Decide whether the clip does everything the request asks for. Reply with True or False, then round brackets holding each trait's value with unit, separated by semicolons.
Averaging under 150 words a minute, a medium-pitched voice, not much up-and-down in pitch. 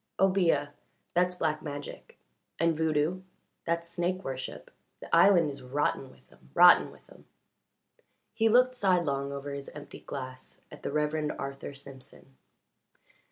False (135 wpm; 150 Hz; 4.0 semitones)